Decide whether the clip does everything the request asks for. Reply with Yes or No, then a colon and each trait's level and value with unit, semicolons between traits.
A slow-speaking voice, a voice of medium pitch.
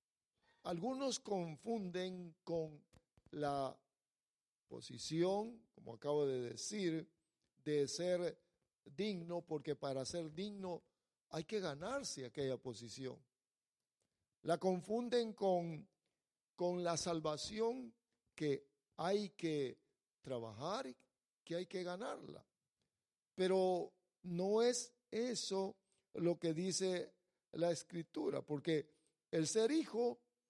Yes: slow, 95 wpm; medium, 175 Hz